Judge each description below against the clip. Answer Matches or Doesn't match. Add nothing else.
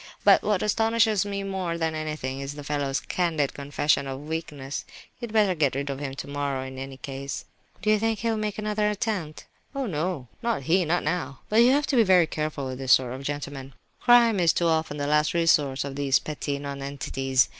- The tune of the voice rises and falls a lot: Matches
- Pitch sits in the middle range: Matches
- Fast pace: Matches